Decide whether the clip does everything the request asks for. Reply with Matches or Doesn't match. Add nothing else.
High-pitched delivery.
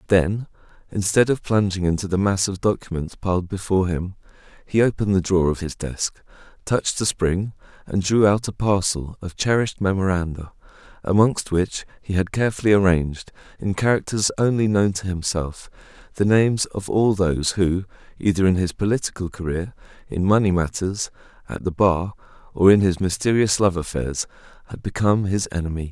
Doesn't match